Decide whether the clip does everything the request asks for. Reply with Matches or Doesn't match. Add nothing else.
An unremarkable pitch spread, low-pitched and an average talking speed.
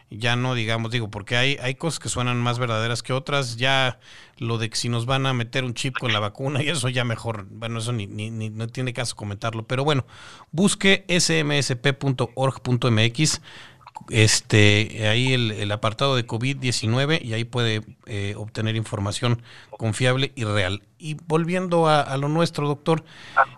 Matches